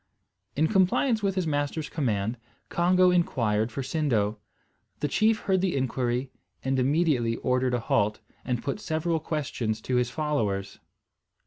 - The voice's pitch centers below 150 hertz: Yes, low, 135 Hz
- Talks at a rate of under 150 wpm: Yes, average, 140 wpm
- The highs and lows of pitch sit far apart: Yes, wide, 5.8 semitones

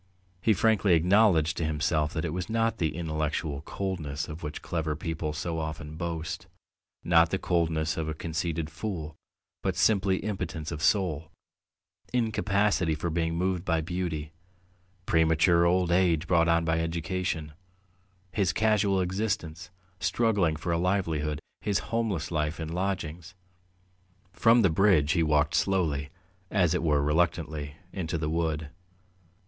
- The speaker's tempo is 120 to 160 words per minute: Yes, average, 140 wpm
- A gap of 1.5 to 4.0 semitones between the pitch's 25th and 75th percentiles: Yes, average, 3.1 semitones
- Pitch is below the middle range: Yes, very low, 85 Hz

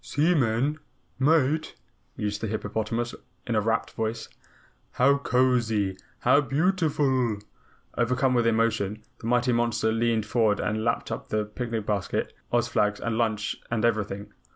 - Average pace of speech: No, slow, 130 wpm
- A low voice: Yes, low, 115 Hz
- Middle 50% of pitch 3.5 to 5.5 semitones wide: No, average, 2.9 semitones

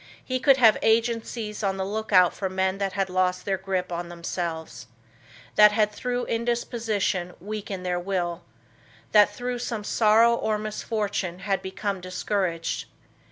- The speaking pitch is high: Yes, high, 200 Hz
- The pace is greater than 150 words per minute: No, average, 145 wpm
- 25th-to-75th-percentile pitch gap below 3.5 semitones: Yes, average, 3.1 semitones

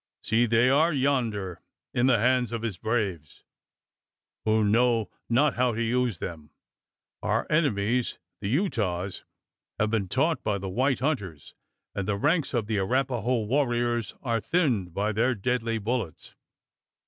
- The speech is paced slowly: No, average, 145 wpm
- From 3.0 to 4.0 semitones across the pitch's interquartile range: Yes, average, 3.7 semitones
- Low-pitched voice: Yes, low, 115 Hz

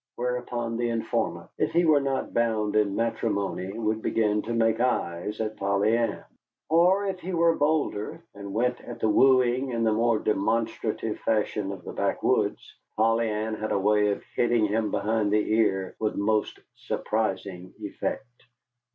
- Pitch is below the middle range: Yes, low, 110 Hz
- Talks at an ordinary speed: Yes, average, 160 wpm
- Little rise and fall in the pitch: Yes, narrow, 2.3 semitones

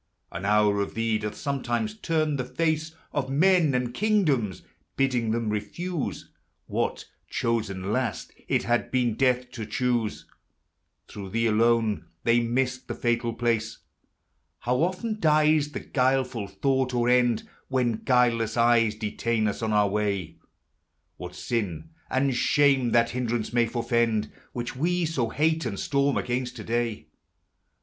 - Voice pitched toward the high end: No, low, 120 Hz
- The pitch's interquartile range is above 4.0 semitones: No, average, 3.4 semitones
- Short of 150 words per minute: Yes, average, 140 wpm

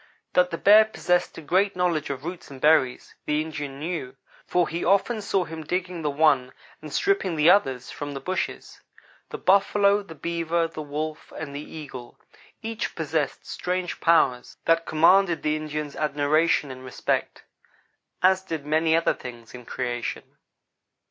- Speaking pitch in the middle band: Yes, medium, 160 Hz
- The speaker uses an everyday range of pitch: Yes, average, 3.8 semitones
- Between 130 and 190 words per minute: Yes, average, 160 wpm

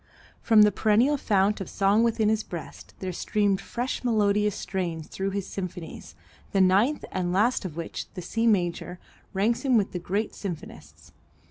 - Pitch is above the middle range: Yes, high, 200 Hz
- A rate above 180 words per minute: No, average, 165 wpm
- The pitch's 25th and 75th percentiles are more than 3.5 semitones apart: No, average, 3.1 semitones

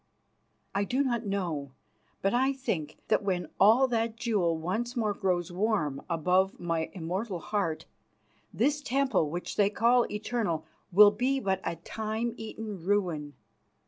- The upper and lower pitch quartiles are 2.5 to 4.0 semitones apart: No, average, 4.9 semitones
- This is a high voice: Yes, high, 200 Hz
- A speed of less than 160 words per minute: Yes, average, 145 wpm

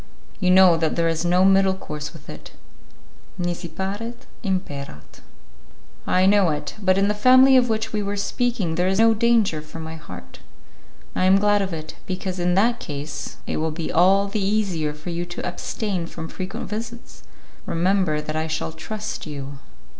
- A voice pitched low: No, medium, 185 Hz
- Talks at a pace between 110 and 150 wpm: No, average, 180 wpm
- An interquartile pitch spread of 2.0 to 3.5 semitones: No, average, 4.2 semitones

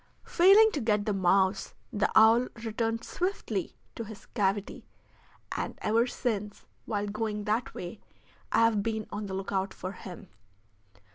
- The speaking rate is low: No, average, 145 wpm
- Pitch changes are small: Yes, narrow, 2.3 semitones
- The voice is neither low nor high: No, high, 215 Hz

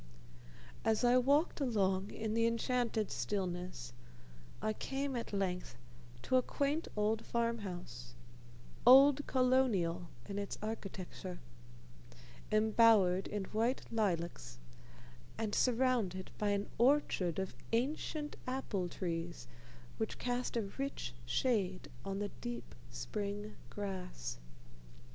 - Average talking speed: No, slow, 110 wpm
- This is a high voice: Yes, high, 215 Hz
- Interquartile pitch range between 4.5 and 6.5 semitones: Yes, average, 4.8 semitones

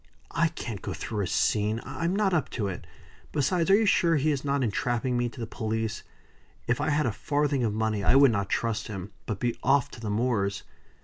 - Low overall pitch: Yes, low, 120 Hz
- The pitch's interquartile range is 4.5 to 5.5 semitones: Yes, average, 5.1 semitones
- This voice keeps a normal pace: No, fast, 225 wpm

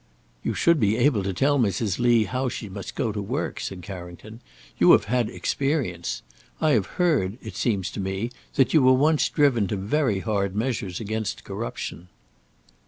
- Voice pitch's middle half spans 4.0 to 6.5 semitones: Yes, average, 5.1 semitones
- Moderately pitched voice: No, low, 110 Hz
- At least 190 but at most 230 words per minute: No, average, 175 wpm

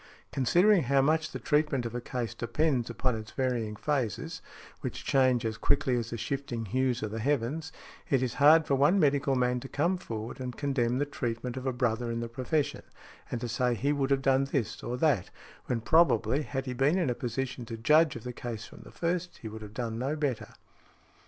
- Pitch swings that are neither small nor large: Yes, average, 3.4 semitones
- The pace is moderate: No, fast, 215 wpm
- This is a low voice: Yes, low, 130 Hz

